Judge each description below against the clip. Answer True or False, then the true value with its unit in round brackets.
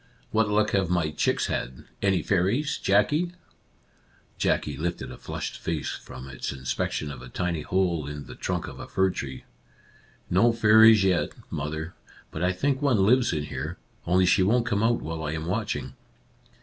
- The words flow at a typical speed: True (185 wpm)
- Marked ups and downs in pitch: True (5.7 semitones)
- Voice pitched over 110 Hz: False (90 Hz)